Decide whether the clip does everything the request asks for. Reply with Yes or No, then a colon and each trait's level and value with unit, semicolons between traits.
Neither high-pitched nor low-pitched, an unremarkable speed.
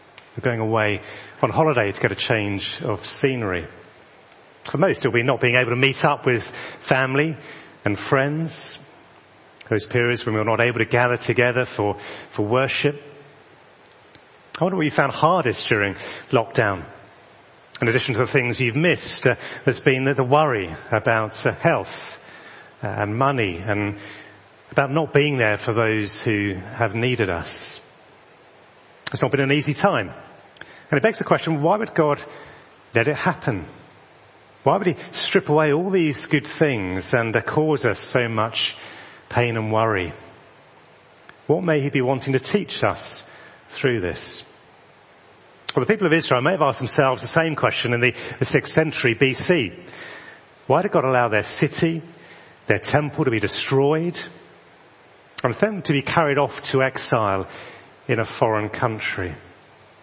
No: low, 130 Hz; average, 160 wpm